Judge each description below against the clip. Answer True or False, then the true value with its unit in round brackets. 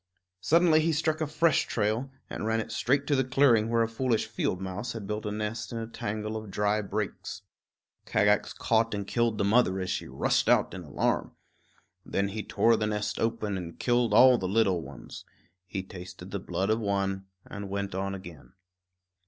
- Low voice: True (105 Hz)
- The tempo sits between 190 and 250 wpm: True (195 wpm)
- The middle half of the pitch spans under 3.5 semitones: True (3.1 semitones)